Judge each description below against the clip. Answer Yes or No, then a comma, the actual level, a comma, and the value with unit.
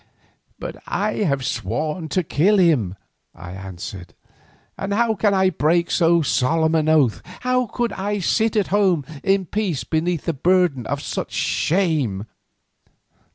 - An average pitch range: No, wide, 5.7 semitones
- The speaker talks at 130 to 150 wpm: Yes, average, 145 wpm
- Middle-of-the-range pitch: Yes, medium, 170 Hz